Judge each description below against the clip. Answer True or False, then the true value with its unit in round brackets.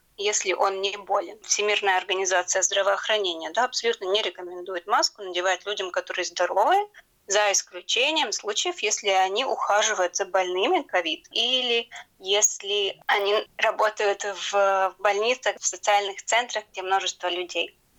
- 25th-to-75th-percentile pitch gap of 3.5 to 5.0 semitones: False (3.1 semitones)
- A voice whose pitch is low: False (200 Hz)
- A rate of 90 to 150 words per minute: True (125 wpm)